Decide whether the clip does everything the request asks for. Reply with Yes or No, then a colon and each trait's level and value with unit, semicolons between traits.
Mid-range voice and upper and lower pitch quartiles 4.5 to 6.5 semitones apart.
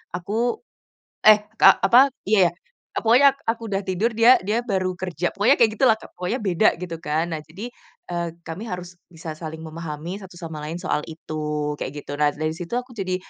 Yes: medium, 180 Hz; average, 5.2 semitones